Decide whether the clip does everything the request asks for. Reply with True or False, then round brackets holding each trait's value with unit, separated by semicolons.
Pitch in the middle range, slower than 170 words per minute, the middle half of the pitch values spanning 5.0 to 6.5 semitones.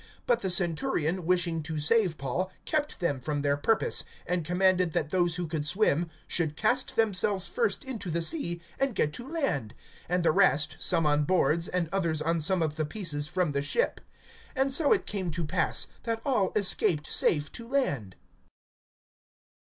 False (175 Hz; 175 wpm; 5.4 semitones)